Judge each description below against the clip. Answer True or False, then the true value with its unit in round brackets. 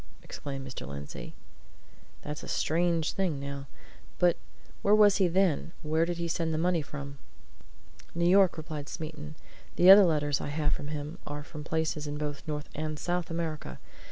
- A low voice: False (155 Hz)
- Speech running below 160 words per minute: False (170 wpm)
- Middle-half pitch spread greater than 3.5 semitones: False (2.7 semitones)